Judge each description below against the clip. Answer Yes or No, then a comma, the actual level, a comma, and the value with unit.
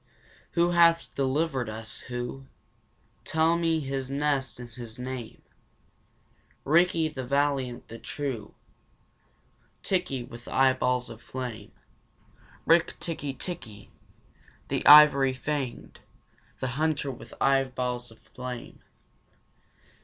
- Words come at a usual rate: No, slow, 100 wpm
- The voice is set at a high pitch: No, low, 135 Hz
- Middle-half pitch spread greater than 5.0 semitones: No, average, 3.5 semitones